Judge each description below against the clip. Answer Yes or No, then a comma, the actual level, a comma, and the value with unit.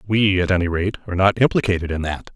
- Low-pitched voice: Yes, very low, 95 Hz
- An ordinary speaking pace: No, fast, 230 wpm